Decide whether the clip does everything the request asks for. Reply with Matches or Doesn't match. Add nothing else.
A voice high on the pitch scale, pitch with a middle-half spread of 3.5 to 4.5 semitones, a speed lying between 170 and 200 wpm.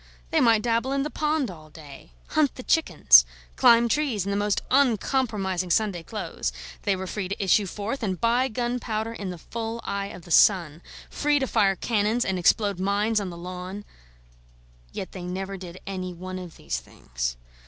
Matches